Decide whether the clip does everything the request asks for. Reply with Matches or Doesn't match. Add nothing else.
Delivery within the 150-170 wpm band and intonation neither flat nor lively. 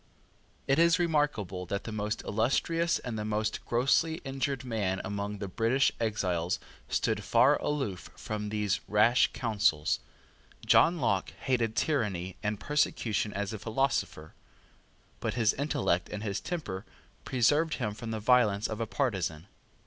Doesn't match